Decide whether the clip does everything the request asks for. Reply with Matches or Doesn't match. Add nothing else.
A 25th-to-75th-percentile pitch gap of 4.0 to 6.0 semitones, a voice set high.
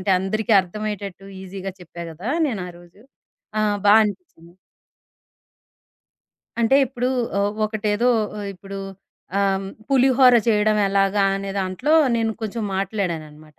Doesn't match